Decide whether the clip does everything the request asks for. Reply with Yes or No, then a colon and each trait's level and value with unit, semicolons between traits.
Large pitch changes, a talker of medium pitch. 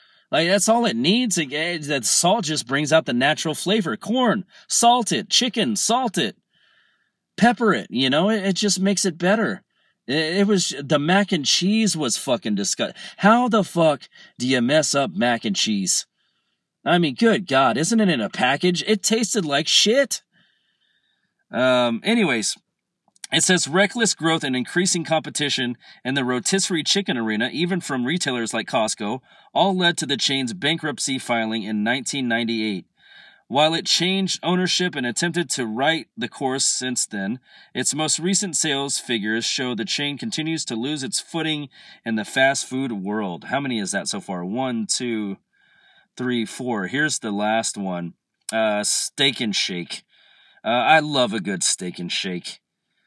Yes: wide, 7.6 semitones; medium, 155 Hz